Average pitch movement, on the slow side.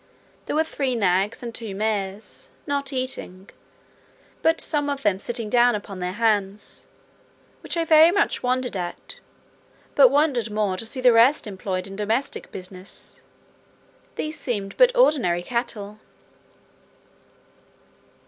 No: wide, 5.7 semitones; slow, 130 wpm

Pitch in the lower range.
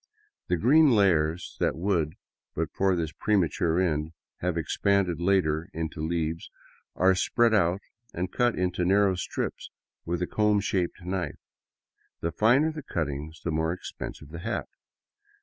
Yes: very low, 90 Hz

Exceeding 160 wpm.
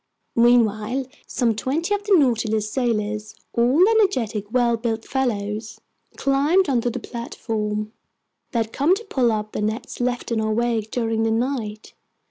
No: average, 140 wpm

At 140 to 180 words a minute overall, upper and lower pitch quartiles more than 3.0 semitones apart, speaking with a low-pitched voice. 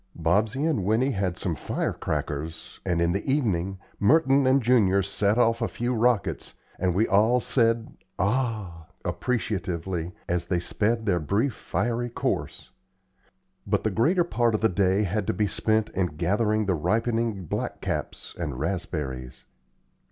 Yes: average, 150 wpm; average, 4.7 semitones; low, 105 Hz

